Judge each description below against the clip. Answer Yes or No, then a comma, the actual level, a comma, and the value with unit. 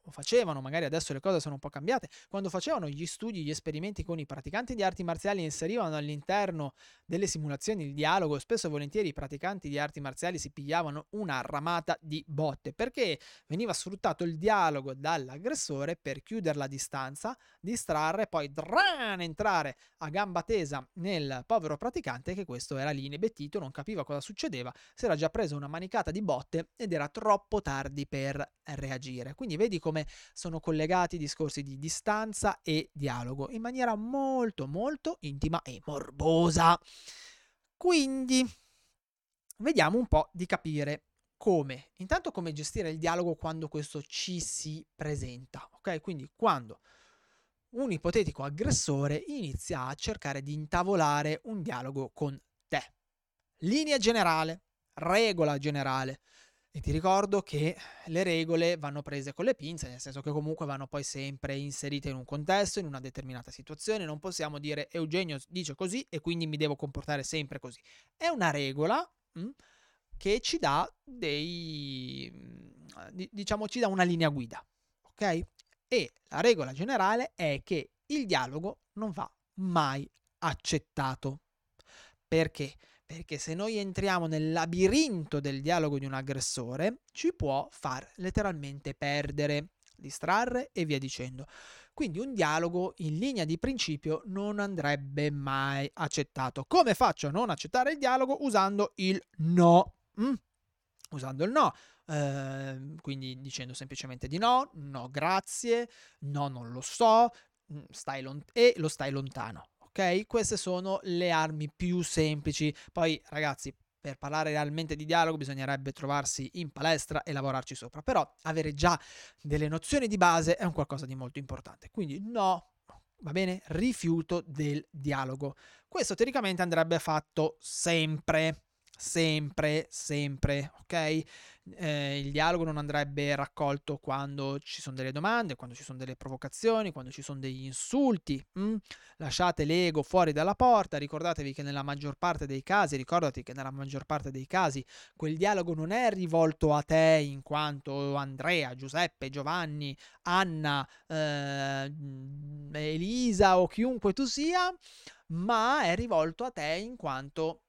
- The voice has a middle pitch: Yes, medium, 155 Hz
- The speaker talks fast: No, average, 145 wpm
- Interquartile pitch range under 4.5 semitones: No, average, 4.9 semitones